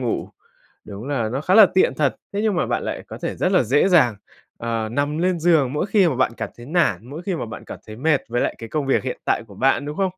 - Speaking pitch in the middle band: Yes, medium, 145 Hz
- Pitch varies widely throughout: Yes, wide, 6.5 semitones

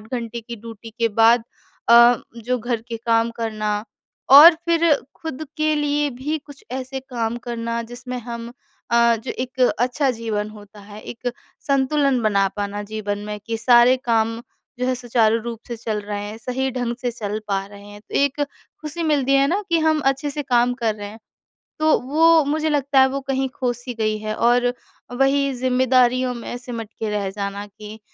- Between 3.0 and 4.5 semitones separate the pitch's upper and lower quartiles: Yes, average, 3.4 semitones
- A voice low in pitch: No, high, 240 Hz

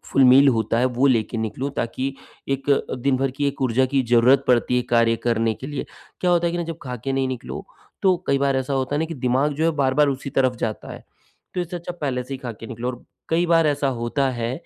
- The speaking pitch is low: Yes, low, 130 Hz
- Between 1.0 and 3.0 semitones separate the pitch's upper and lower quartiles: Yes, narrow, 2.6 semitones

